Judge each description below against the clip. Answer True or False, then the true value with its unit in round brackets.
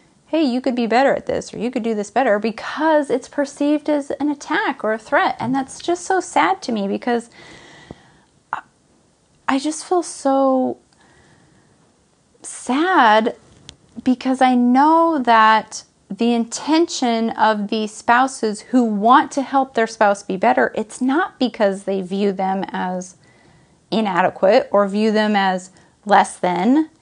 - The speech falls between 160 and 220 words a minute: False (145 wpm)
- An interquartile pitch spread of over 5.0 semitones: True (5.4 semitones)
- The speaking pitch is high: True (240 Hz)